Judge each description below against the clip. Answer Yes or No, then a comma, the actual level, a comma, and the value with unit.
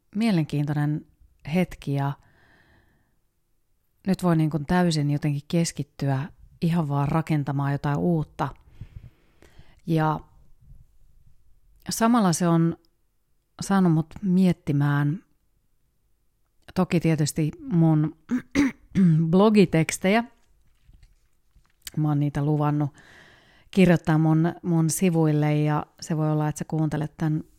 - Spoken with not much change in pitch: No, average, 3.0 semitones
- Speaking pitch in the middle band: Yes, medium, 160 Hz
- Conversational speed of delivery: No, slow, 90 wpm